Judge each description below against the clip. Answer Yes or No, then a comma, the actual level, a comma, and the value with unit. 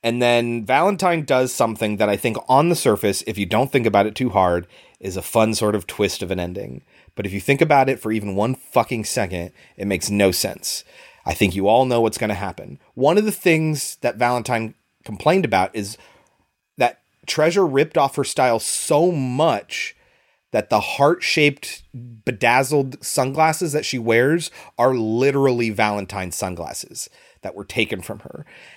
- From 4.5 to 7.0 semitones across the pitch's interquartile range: Yes, average, 5.2 semitones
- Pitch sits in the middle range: No, low, 115 Hz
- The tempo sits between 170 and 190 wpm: Yes, average, 180 wpm